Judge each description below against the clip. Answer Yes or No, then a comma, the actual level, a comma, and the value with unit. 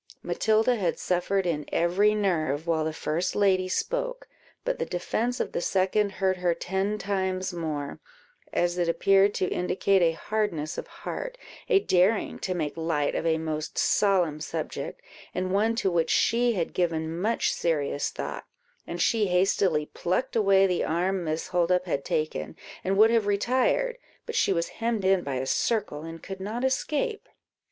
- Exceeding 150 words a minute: Yes, average, 170 wpm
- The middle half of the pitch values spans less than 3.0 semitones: No, average, 4.1 semitones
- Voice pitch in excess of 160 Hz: Yes, medium, 185 Hz